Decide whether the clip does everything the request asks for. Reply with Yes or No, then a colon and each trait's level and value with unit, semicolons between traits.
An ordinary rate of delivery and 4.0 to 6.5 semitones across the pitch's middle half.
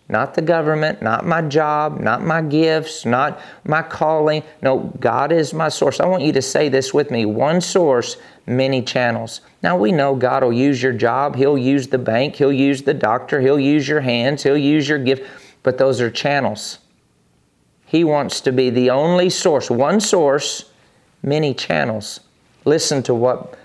No: average, 180 wpm; average, 3.1 semitones